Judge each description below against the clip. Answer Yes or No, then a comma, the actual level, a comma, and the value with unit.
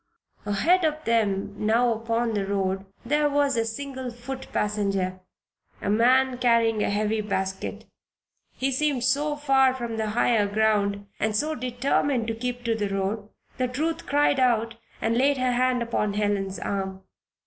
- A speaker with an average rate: Yes, average, 160 wpm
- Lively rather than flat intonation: No, average, 4.0 semitones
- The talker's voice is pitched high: Yes, high, 230 Hz